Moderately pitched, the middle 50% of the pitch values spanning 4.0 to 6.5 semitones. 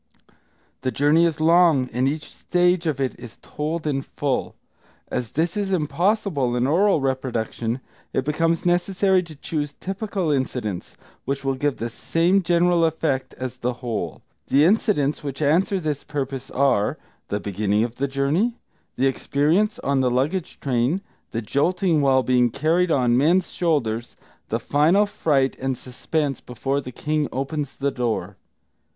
Yes: medium, 145 Hz; average, 4.6 semitones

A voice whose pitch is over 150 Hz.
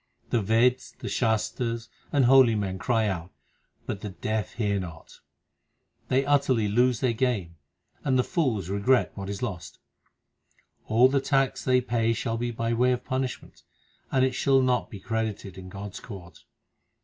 No: low, 115 Hz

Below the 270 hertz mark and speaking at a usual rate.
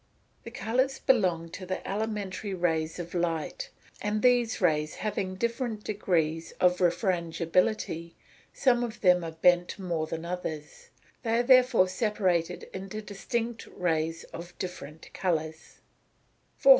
No: medium, 185 Hz; slow, 130 wpm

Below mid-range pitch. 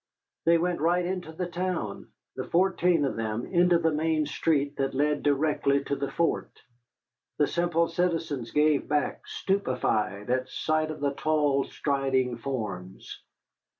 No: medium, 150 Hz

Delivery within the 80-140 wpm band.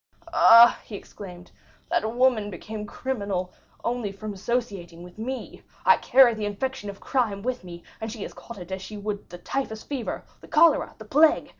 No: average, 180 wpm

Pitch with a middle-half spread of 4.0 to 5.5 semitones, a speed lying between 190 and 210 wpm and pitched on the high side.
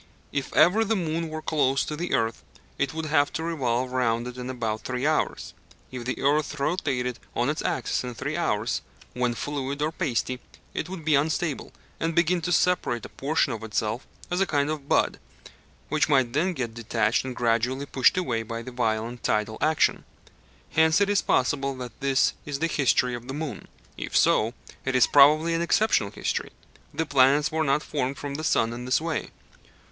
No: average, 4.3 semitones; average, 195 wpm; medium, 140 Hz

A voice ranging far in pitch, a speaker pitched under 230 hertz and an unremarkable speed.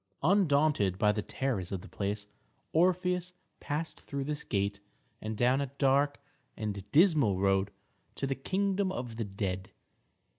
Yes: wide, 7.6 semitones; low, 135 Hz; average, 145 wpm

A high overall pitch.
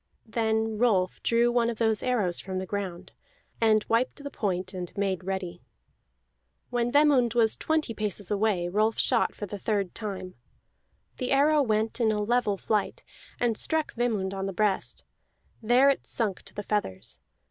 Yes: high, 215 Hz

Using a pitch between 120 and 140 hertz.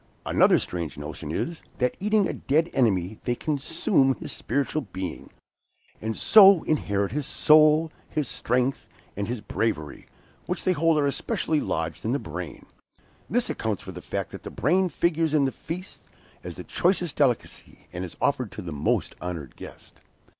Yes: low, 135 Hz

